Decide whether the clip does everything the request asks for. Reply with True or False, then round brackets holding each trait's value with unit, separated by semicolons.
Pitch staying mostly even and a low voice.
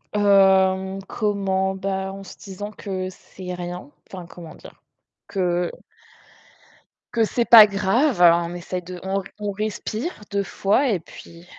False (2.0 semitones; 190 Hz)